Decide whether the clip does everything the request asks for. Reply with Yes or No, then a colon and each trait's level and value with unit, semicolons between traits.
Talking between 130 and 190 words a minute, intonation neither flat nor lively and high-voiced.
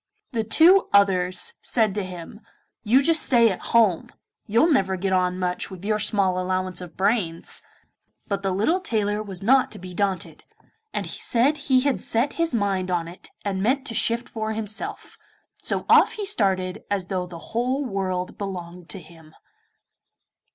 Yes: average, 170 wpm; average, 4.1 semitones; high, 200 Hz